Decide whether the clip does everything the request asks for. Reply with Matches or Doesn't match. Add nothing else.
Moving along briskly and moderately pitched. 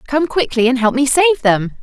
Doesn't match